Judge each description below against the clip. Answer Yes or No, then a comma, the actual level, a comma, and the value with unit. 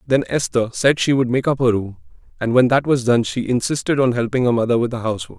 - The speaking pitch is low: Yes, low, 125 Hz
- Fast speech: Yes, fast, 255 wpm